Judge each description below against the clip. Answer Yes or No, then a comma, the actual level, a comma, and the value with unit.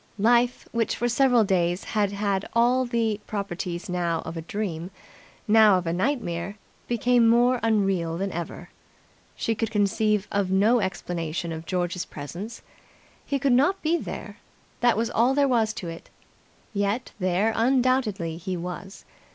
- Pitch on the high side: Yes, high, 205 Hz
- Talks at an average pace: Yes, average, 150 wpm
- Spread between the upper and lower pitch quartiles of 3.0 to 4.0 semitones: No, average, 4.9 semitones